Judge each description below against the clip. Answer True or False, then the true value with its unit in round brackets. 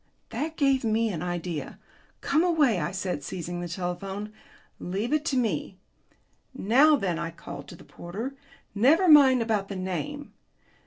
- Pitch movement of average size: False (7.5 semitones)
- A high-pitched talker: True (205 Hz)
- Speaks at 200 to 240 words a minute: False (155 wpm)